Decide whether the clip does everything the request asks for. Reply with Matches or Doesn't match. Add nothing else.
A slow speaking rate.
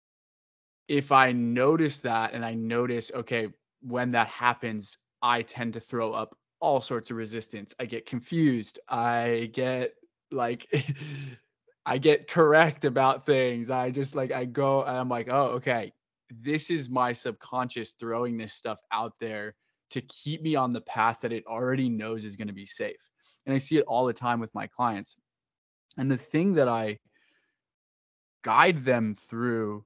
Doesn't match